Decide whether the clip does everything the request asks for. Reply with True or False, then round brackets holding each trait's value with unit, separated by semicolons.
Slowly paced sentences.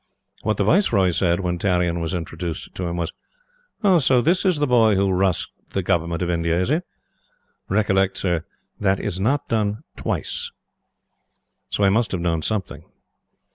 False (165 wpm)